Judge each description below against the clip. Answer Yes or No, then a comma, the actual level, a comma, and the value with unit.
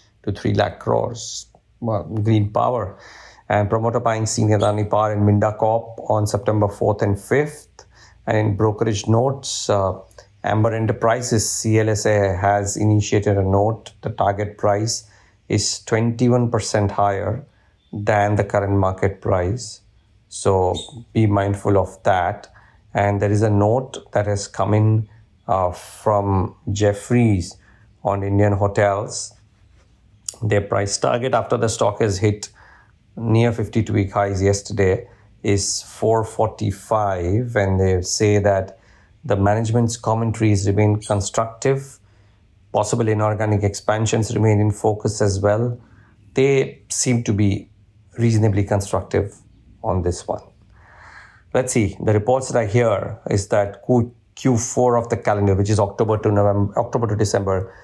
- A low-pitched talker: Yes, low, 105 Hz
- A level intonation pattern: Yes, narrow, 1.8 semitones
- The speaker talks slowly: Yes, slow, 130 wpm